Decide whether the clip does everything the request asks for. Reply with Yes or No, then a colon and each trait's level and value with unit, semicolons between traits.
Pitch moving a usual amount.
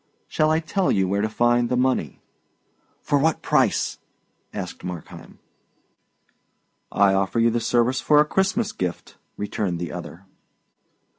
No: wide, 7.4 semitones